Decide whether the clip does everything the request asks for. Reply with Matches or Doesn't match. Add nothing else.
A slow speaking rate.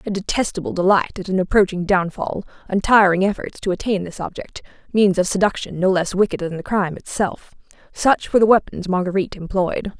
Doesn't match